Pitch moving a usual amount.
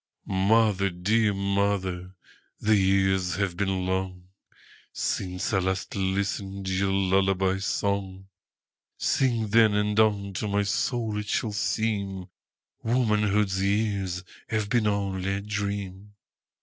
No: narrow, 1.6 semitones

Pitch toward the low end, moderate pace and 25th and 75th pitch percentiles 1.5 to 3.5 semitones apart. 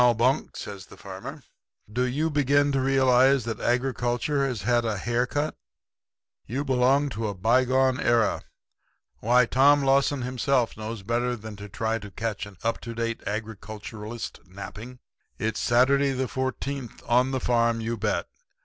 Yes: low, 120 Hz; average, 160 wpm; average, 2.9 semitones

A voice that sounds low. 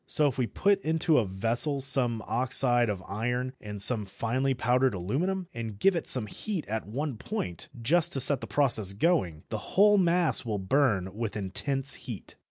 Yes: low, 125 Hz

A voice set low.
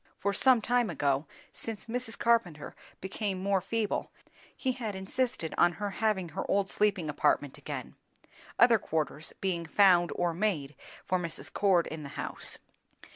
No: high, 190 Hz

